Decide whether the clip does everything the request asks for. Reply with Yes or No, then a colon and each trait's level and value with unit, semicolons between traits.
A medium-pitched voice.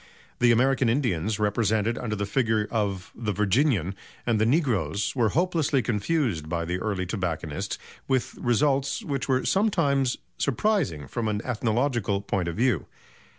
No: low, 115 Hz